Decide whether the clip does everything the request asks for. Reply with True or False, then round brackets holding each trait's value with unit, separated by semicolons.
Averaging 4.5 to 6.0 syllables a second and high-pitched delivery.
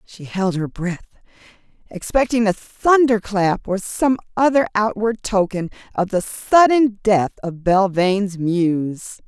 False (4.1 syllables/s; 205 Hz)